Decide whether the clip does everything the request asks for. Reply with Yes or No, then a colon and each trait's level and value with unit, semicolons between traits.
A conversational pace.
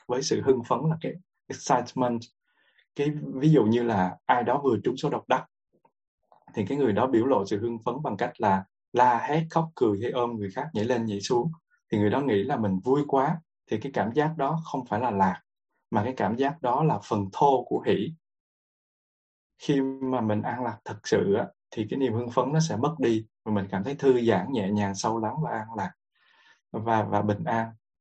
Yes: average, 220 wpm